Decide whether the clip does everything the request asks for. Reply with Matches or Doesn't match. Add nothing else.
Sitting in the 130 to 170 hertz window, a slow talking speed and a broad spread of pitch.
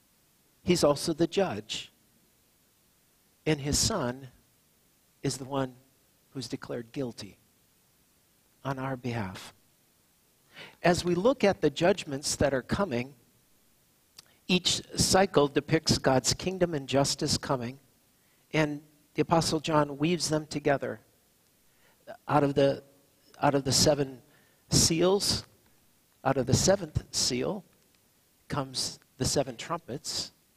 Doesn't match